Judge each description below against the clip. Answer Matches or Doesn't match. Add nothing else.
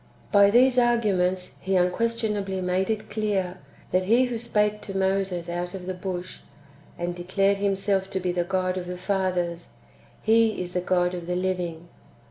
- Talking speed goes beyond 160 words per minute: Matches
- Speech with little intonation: Matches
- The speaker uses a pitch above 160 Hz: Matches